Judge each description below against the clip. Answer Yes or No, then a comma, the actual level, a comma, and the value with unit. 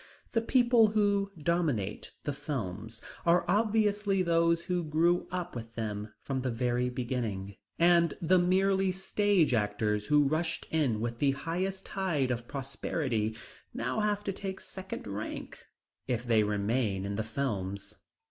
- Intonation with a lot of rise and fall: Yes, wide, 8.6 semitones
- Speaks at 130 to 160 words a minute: Yes, average, 145 wpm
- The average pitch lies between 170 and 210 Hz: No, medium, 150 Hz